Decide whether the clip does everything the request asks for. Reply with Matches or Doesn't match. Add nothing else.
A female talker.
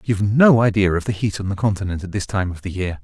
Doesn't match